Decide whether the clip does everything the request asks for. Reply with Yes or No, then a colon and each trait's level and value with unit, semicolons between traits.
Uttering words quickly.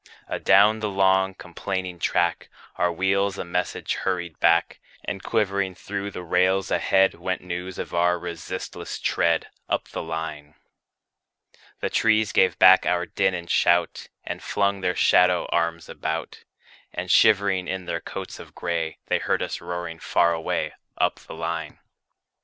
No: average, 150 wpm